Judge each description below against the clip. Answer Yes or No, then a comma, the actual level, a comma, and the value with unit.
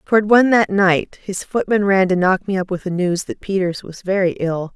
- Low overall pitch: No, high, 190 Hz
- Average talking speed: No, fast, 240 wpm